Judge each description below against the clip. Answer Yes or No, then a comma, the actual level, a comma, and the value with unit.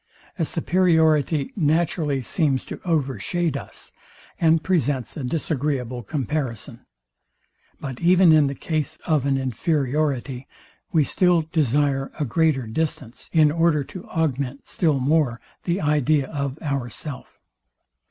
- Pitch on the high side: No, medium, 150 Hz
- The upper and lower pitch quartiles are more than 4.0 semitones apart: No, average, 3.2 semitones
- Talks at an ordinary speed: No, slow, 120 wpm